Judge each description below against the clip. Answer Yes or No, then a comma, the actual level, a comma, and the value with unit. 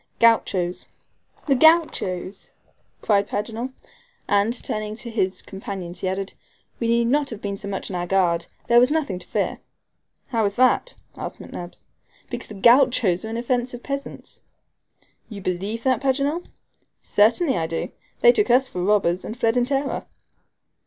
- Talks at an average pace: Yes, average, 155 wpm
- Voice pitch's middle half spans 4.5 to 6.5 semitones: Yes, average, 4.8 semitones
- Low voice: No, high, 225 Hz